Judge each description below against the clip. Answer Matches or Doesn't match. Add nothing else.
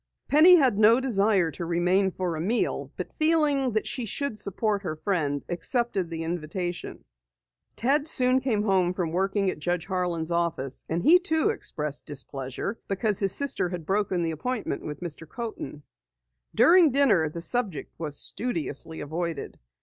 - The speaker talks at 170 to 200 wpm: Doesn't match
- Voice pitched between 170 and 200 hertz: Matches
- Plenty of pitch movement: Matches